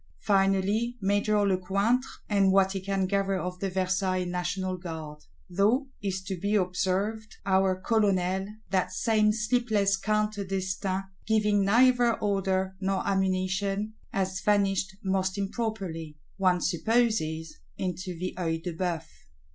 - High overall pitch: Yes, high, 195 Hz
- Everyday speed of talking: No, slow, 130 wpm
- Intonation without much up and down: Yes, narrow, 2.0 semitones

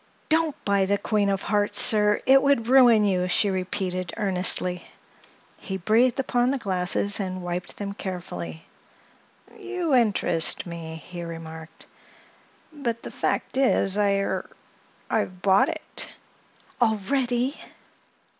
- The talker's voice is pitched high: Yes, high, 200 Hz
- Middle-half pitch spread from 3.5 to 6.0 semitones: Yes, average, 5.0 semitones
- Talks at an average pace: No, slow, 115 wpm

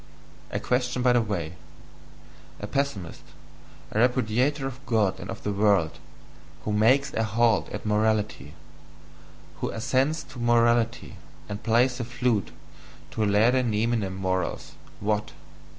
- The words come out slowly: Yes, slow, 130 wpm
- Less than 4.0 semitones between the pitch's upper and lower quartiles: Yes, average, 3.1 semitones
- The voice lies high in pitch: No, low, 115 Hz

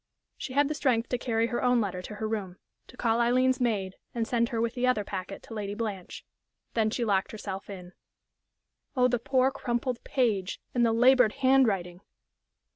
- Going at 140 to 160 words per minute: No, average, 195 wpm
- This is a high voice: Yes, high, 230 Hz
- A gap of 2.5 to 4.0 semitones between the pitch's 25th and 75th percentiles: Yes, average, 3.5 semitones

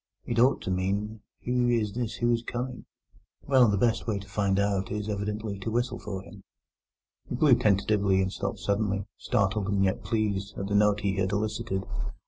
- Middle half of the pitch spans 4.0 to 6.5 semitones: No, narrow, 2.6 semitones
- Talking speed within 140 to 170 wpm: No, average, 190 wpm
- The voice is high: No, low, 105 Hz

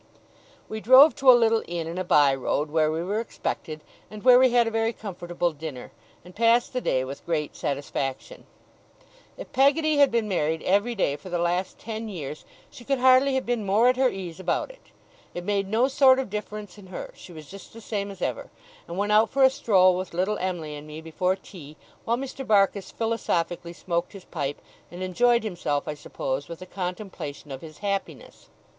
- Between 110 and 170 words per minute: No, fast, 205 wpm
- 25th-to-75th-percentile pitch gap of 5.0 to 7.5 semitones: Yes, wide, 5.5 semitones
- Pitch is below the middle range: No, high, 190 Hz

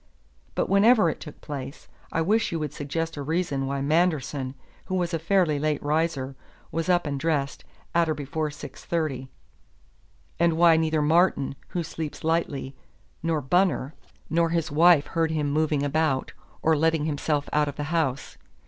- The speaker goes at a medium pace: Yes, average, 165 wpm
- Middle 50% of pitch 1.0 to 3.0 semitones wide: Yes, narrow, 2.6 semitones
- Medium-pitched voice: Yes, medium, 155 Hz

